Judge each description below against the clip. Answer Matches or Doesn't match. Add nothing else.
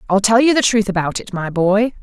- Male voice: Doesn't match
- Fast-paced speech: Matches